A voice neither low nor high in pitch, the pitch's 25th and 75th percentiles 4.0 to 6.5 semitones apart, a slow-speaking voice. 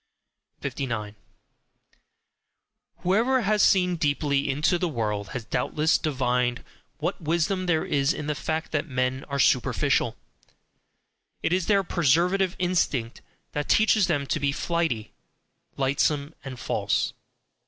Yes: medium, 150 Hz; average, 5.0 semitones; slow, 120 wpm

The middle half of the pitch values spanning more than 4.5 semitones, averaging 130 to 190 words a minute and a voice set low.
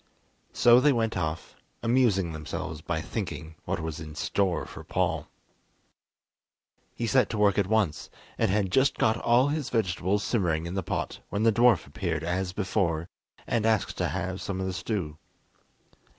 Yes: average, 4.9 semitones; average, 165 wpm; very low, 95 Hz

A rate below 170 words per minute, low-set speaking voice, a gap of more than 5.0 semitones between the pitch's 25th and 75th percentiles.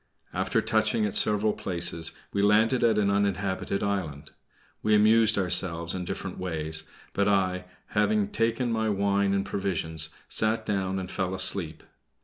No: average, 145 wpm; low, 100 Hz; narrow, 2.6 semitones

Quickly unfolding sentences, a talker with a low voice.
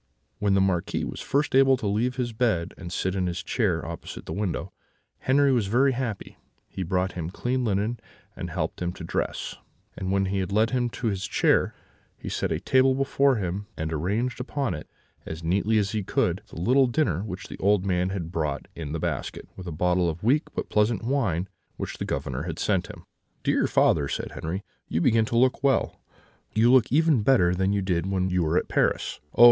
Yes: fast, 210 wpm; low, 100 Hz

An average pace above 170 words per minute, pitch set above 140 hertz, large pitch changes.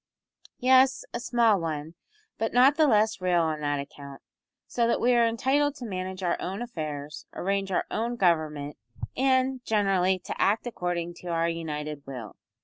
No: average, 165 wpm; high, 190 Hz; wide, 7.2 semitones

